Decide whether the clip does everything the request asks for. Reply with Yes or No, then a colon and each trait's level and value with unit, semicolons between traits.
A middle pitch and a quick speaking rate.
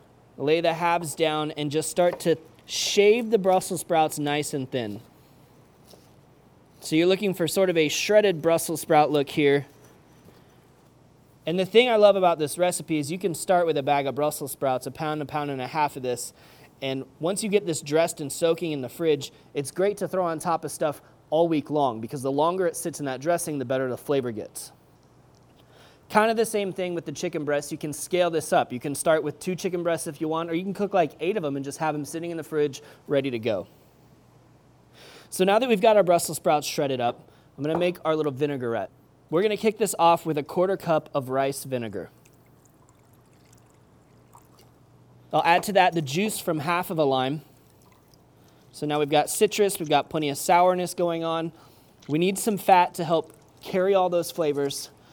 Yes: medium, 160 Hz; fast, 210 wpm